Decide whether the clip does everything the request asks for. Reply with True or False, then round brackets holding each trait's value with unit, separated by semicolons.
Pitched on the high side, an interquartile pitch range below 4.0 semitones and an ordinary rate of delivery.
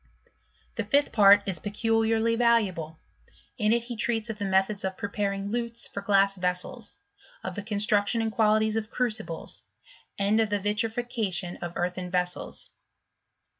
True (210 Hz; 2.5 semitones; 145 wpm)